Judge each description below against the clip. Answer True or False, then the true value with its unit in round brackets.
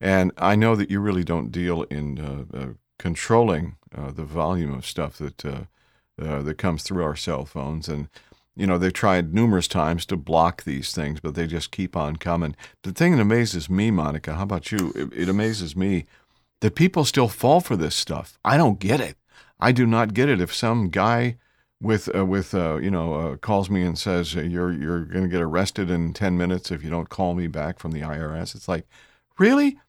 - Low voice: True (90 Hz)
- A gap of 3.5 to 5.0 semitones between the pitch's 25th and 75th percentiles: True (3.8 semitones)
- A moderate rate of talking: False (215 wpm)